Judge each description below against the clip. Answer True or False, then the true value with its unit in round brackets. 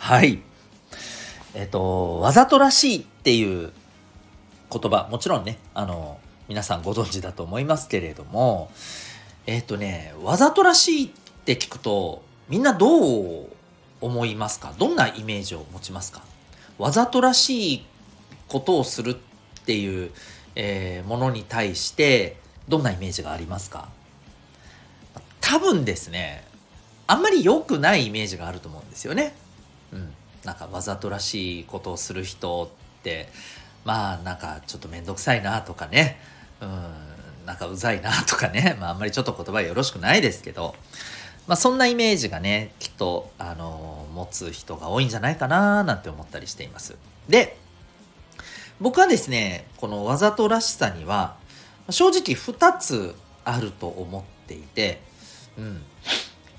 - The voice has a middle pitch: False (100 Hz)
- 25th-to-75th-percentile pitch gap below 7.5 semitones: True (5.9 semitones)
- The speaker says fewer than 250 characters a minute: False (300 characters per minute)